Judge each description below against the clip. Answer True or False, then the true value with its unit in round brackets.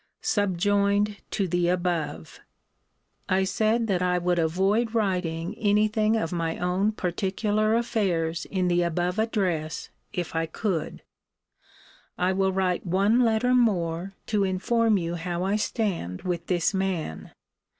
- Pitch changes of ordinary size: True (3.3 semitones)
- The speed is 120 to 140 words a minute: True (135 wpm)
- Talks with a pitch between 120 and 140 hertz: False (185 Hz)